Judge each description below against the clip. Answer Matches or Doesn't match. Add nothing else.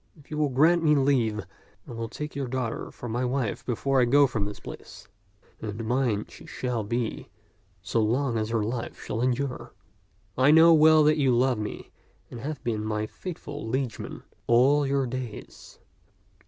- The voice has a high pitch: Doesn't match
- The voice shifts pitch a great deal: Doesn't match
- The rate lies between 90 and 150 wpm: Doesn't match